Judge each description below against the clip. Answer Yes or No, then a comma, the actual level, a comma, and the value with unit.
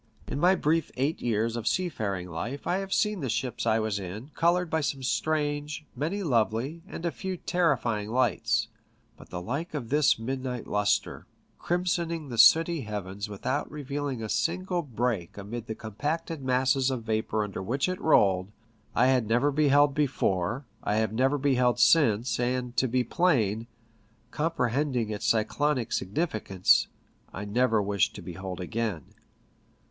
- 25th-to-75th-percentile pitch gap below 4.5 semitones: No, wide, 5.6 semitones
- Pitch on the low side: Yes, low, 125 Hz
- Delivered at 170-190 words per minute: No, average, 160 wpm